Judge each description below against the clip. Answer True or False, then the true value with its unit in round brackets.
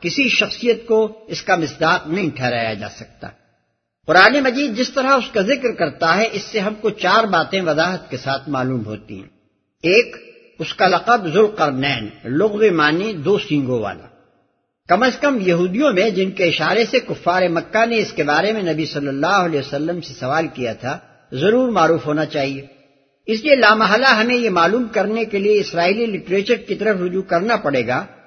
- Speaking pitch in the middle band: True (180 Hz)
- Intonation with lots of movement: True (7.3 semitones)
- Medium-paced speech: True (185 wpm)